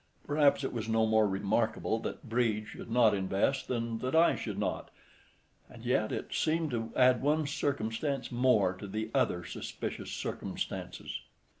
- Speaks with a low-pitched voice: Yes, low, 115 Hz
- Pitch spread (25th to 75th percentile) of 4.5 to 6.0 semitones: No, average, 3.5 semitones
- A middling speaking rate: Yes, average, 150 wpm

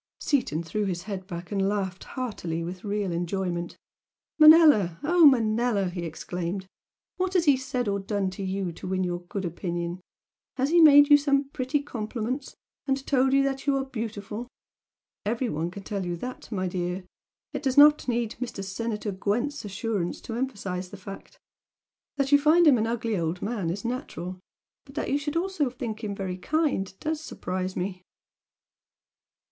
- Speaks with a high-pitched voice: Yes, high, 215 Hz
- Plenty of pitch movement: Yes, wide, 6.4 semitones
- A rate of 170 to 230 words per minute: Yes, average, 175 wpm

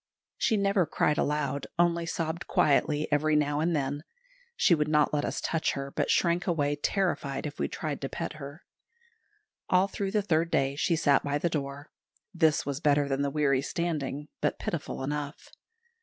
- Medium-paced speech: Yes, average, 180 wpm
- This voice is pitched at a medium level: Yes, medium, 150 Hz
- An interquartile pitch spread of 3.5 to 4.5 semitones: No, average, 2.8 semitones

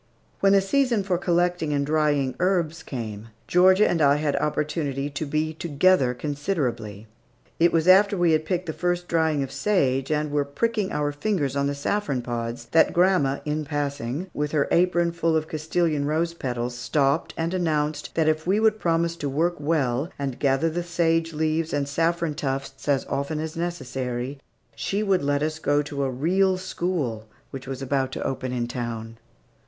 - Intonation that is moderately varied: Yes, average, 3.8 semitones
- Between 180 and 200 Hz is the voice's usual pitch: No, medium, 155 Hz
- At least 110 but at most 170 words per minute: No, average, 180 wpm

